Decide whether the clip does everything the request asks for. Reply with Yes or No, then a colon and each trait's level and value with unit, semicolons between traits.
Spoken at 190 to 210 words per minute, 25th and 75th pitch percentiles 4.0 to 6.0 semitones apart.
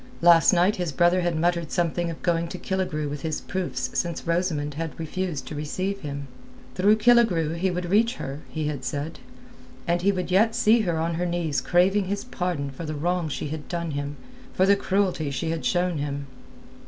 No: average, 195 wpm; average, 3.4 semitones